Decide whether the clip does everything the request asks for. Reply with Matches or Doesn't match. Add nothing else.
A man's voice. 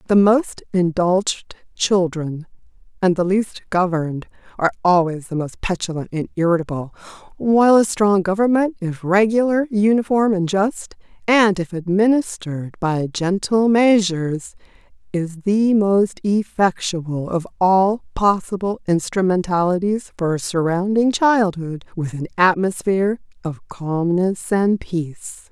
Doesn't match